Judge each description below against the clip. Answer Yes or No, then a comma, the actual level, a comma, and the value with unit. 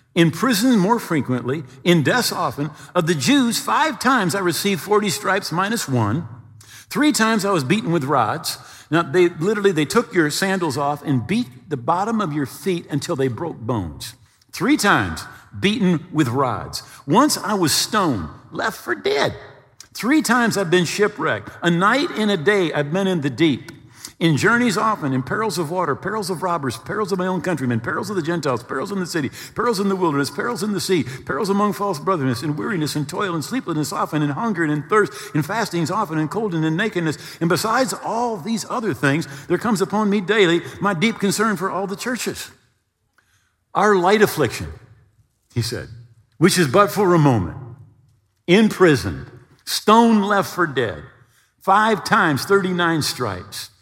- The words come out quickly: No, average, 185 wpm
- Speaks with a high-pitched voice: No, medium, 180 Hz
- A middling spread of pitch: No, wide, 6.1 semitones